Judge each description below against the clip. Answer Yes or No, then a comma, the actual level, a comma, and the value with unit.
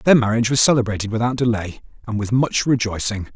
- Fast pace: No, average, 180 wpm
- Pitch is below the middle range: Yes, low, 115 Hz